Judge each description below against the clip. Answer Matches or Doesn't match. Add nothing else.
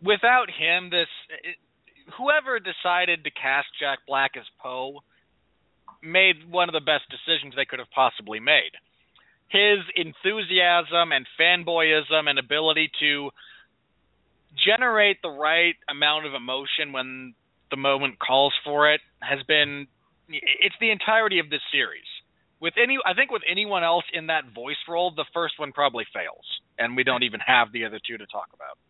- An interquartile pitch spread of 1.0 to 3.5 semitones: Doesn't match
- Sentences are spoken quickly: Doesn't match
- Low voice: Doesn't match